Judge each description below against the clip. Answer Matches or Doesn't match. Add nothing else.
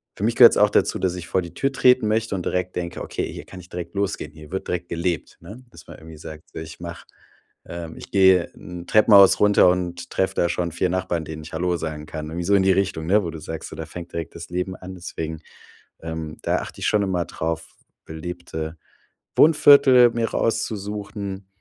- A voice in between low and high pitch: Doesn't match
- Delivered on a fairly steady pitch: Doesn't match